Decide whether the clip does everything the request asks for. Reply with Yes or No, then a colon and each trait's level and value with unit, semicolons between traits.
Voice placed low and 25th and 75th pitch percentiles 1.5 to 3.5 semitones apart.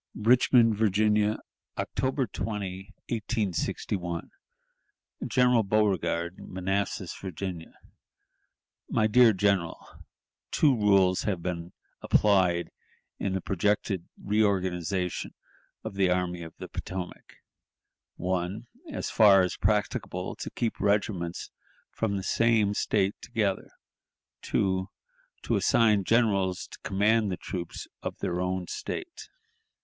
Yes: low, 100 Hz; average, 2.8 semitones